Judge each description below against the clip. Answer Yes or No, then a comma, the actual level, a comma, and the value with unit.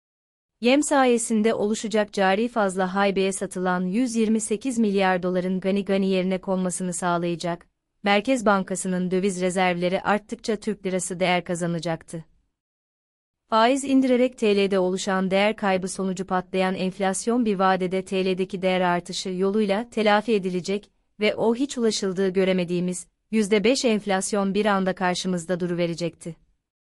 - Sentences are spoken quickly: No, average, 120 wpm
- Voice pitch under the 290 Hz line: Yes, high, 190 Hz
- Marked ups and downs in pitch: No, narrow, 2.5 semitones